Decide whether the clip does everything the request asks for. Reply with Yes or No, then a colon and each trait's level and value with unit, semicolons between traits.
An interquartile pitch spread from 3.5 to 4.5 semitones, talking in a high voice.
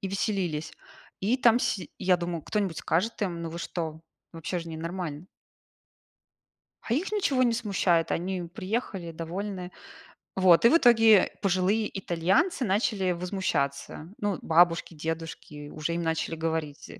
No: average, 4.0 semitones; medium, 180 Hz